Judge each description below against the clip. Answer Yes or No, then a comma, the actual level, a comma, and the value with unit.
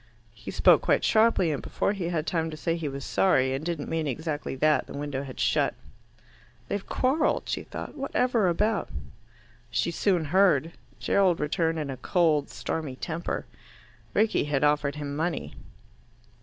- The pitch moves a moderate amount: Yes, average, 4.0 semitones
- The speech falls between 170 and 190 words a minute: No, average, 160 wpm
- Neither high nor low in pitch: Yes, medium, 160 Hz